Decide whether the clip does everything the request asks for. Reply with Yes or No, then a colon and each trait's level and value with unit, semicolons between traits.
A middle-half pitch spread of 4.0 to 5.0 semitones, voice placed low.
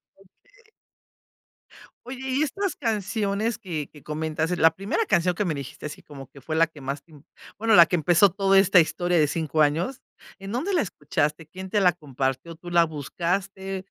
No: average, 4.4 semitones; medium, 175 Hz